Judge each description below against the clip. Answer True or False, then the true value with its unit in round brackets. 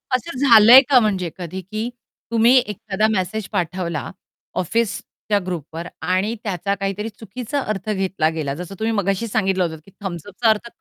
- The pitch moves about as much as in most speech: True (3.4 semitones)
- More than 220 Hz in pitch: False (200 Hz)